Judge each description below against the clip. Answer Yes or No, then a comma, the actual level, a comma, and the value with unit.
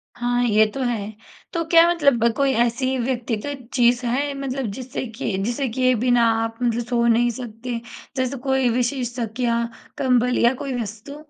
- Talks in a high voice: Yes, high, 245 Hz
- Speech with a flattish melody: Yes, narrow, 2.1 semitones